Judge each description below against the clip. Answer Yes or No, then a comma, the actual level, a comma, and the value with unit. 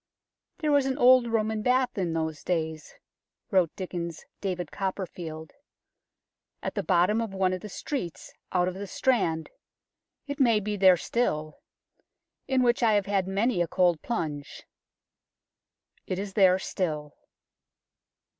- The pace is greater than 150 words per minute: No, average, 145 wpm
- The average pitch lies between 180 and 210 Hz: Yes, high, 190 Hz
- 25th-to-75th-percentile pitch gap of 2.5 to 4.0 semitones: No, average, 4.9 semitones